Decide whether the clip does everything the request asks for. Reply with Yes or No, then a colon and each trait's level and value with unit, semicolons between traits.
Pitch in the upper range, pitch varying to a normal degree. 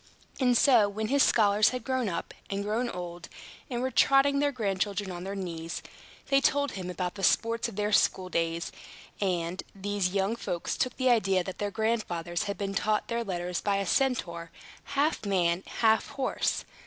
Yes: high, 205 Hz; average, 4.6 semitones